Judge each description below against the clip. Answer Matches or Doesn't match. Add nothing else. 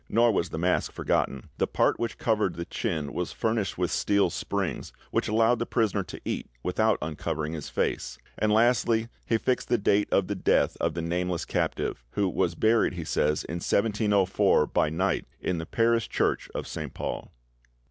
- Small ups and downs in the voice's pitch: Doesn't match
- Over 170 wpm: Matches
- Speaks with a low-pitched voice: Matches